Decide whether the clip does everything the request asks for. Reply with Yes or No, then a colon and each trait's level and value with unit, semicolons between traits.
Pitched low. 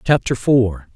Yes: low, 115 Hz